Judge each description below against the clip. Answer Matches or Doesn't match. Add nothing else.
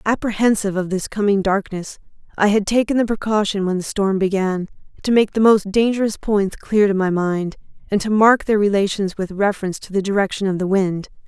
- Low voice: Doesn't match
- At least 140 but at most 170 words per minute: Doesn't match